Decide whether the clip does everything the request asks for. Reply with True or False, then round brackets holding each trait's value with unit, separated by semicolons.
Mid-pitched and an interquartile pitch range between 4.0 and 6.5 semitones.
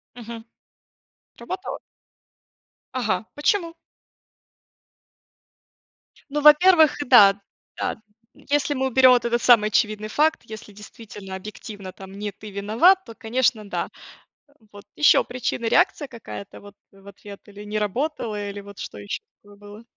False (220 Hz; 4.4 semitones)